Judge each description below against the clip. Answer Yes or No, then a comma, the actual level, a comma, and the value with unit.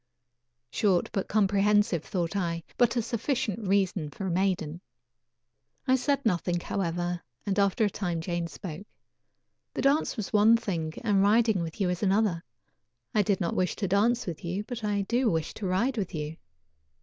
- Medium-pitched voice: No, high, 195 Hz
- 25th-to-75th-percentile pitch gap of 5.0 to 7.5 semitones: No, average, 3.8 semitones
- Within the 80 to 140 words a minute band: No, average, 175 wpm